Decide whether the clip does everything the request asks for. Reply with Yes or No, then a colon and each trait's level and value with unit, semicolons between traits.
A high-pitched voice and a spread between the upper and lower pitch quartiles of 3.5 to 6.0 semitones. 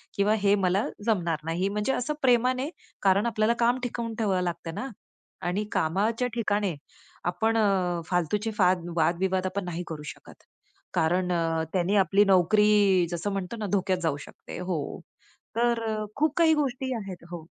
Yes: high, 195 Hz; average, 4.2 semitones